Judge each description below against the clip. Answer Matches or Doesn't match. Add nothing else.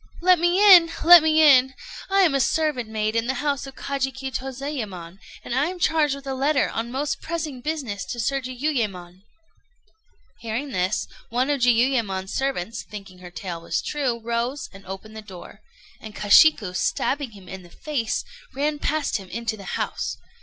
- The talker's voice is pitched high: Matches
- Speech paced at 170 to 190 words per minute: Matches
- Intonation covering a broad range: Matches